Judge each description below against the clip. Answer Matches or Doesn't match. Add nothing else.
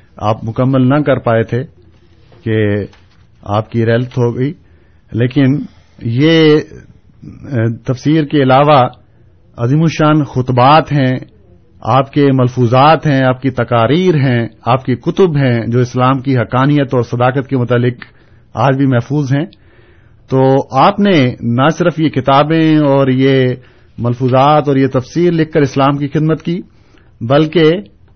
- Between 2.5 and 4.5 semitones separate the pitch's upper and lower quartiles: Matches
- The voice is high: Doesn't match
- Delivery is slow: Doesn't match